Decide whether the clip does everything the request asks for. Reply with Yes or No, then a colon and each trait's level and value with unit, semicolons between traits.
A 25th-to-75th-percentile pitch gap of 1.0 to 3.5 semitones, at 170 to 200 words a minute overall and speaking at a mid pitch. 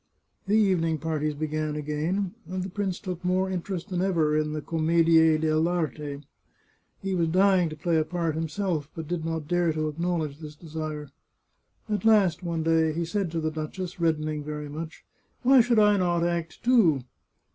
Yes: average, 2.8 semitones; average, 180 wpm; medium, 165 Hz